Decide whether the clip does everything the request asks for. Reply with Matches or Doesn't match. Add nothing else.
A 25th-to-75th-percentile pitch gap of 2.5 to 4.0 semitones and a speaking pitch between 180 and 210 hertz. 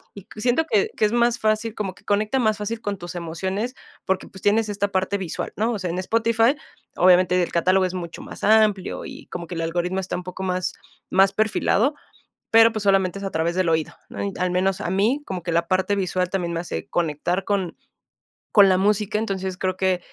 Matches